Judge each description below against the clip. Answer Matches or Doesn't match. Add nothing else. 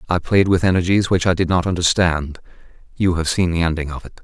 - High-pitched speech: Doesn't match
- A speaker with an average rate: Doesn't match